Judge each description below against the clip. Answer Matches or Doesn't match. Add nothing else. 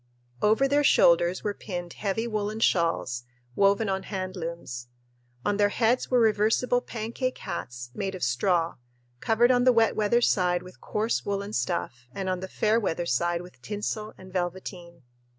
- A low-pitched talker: Doesn't match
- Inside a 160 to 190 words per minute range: Matches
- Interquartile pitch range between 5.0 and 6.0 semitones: Doesn't match